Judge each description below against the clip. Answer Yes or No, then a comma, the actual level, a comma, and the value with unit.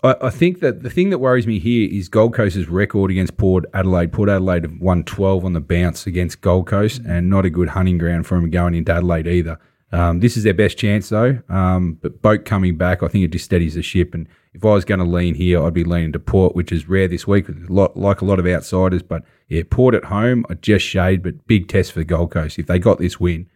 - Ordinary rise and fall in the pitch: Yes, average, 3.0 semitones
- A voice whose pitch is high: No, very low, 90 Hz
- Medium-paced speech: No, fast, 255 wpm